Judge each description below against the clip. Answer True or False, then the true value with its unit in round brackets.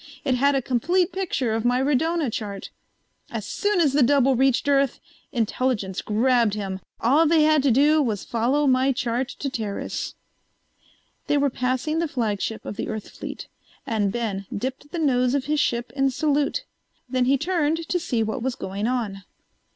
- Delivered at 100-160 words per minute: False (175 wpm)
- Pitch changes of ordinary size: True (4.1 semitones)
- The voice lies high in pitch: True (260 Hz)